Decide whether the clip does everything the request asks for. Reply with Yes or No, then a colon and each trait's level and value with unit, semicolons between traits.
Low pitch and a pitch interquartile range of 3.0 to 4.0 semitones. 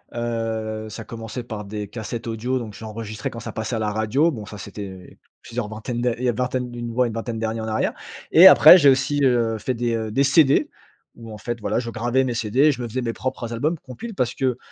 No: low, 115 Hz; narrow, 2.4 semitones